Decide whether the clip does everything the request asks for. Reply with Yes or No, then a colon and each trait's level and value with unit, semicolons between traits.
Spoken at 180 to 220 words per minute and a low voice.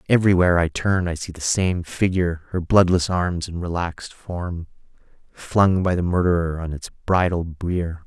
No: average, 155 wpm; very low, 85 Hz